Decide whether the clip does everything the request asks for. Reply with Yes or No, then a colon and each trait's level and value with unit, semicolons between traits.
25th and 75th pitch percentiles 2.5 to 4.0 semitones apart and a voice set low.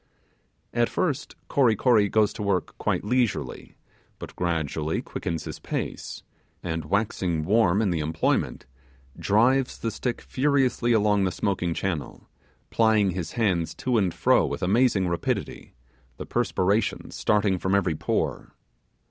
No: average, 4.7 semitones; low, 100 Hz